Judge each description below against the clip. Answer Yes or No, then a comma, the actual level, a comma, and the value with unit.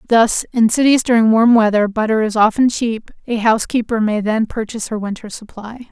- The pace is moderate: Yes, average, 195 wpm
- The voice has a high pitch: Yes, high, 225 Hz